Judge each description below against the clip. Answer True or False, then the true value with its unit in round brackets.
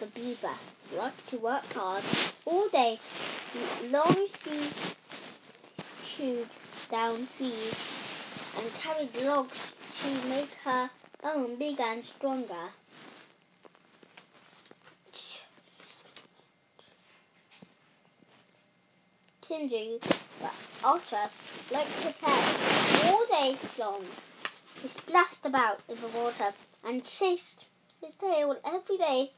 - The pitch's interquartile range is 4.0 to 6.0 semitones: True (4.7 semitones)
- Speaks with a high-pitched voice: True (265 Hz)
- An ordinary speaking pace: False (90 wpm)